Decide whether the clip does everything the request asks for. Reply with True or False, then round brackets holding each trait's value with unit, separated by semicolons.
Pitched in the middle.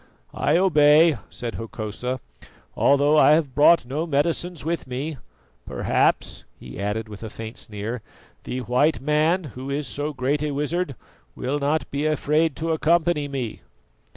True (145 Hz)